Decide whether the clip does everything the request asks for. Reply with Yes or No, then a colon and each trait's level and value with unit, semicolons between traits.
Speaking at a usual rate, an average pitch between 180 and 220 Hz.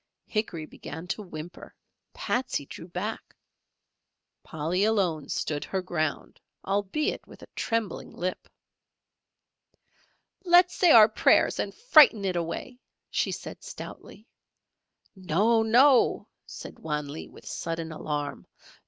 No: slow, 115 wpm; high, 190 Hz